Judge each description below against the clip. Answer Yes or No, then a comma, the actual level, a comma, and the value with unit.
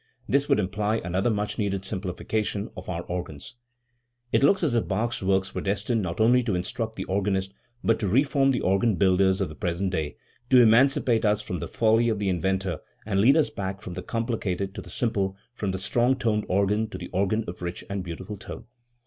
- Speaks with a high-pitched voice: No, low, 100 Hz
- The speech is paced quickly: Yes, fast, 210 wpm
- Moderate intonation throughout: Yes, average, 3.2 semitones